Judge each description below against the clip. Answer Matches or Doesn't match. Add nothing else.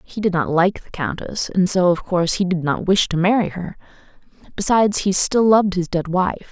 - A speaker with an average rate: Doesn't match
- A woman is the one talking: Matches